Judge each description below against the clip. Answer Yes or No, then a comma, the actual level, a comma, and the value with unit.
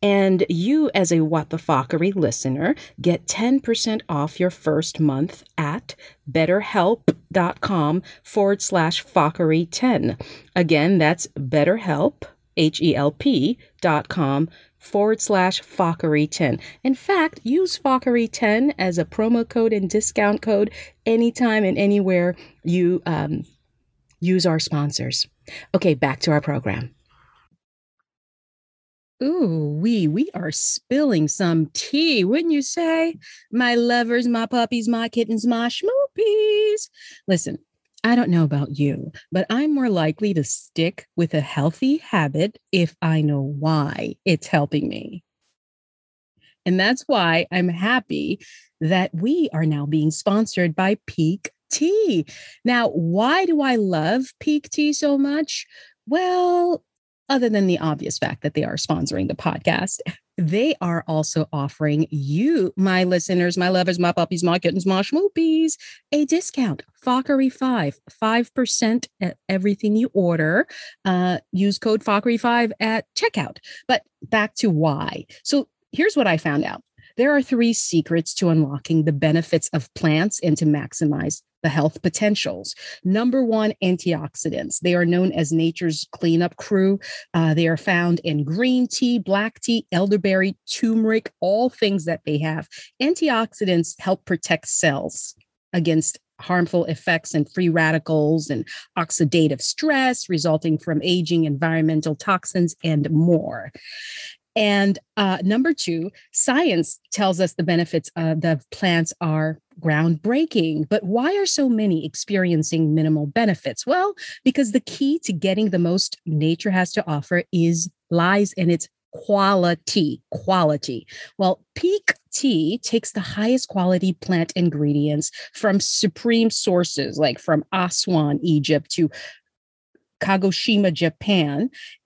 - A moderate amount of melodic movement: No, wide, 6.2 semitones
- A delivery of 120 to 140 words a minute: Yes, slow, 135 wpm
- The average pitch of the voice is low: No, medium, 185 Hz